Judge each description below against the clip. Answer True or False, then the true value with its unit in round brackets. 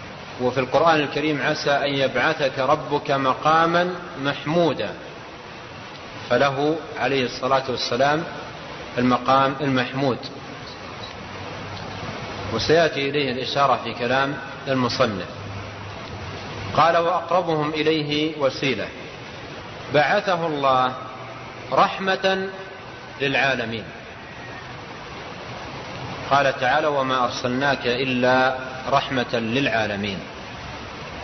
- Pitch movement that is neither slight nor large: True (3.2 semitones)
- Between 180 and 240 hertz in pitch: False (135 Hz)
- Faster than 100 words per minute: False (70 wpm)